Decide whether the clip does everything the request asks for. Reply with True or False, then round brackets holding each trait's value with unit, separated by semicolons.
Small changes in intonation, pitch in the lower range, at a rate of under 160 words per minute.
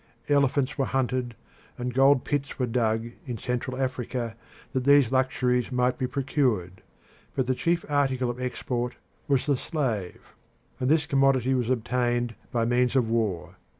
True (1.9 semitones; 125 Hz; 150 wpm)